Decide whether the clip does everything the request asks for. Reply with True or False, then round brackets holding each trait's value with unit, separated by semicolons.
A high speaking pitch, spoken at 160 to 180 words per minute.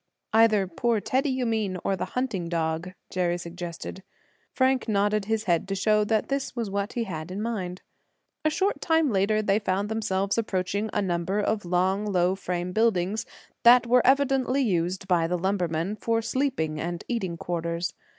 True (200 Hz; 170 wpm)